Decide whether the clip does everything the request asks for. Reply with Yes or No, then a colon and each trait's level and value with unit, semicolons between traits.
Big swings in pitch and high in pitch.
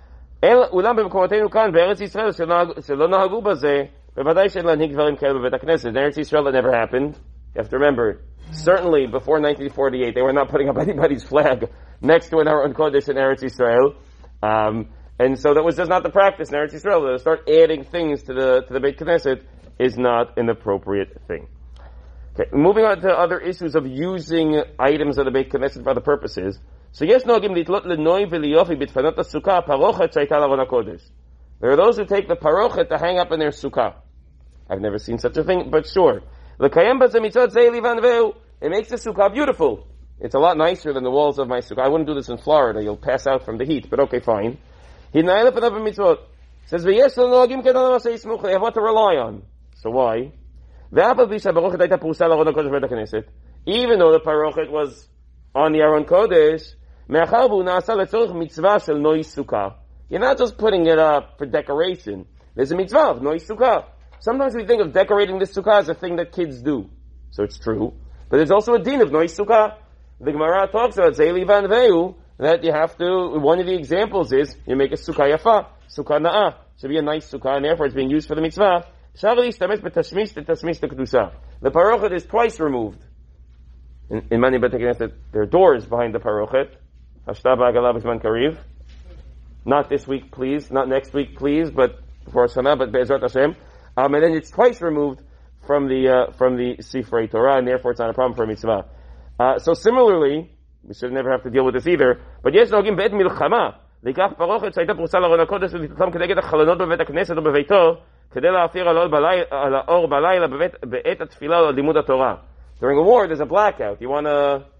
No: wide, 7.0 semitones; medium, 150 Hz